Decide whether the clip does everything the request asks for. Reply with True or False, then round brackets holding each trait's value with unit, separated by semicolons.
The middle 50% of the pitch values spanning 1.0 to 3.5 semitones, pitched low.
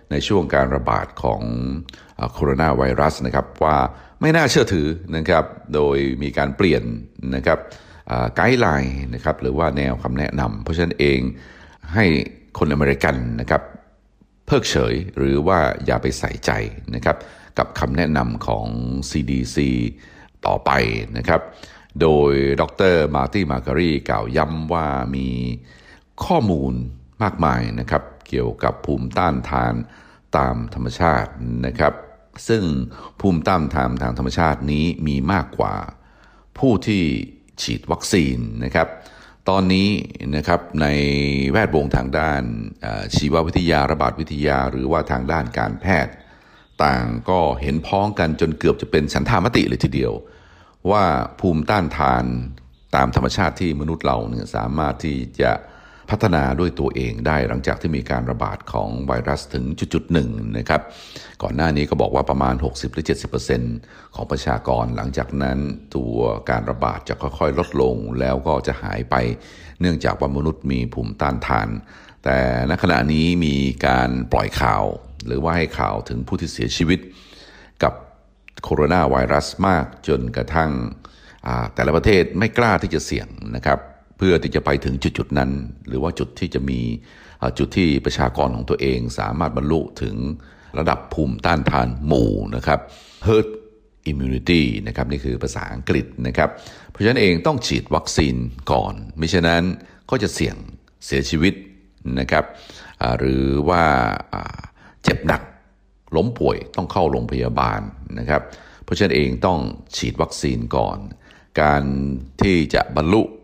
False (4.2 semitones; 70 Hz)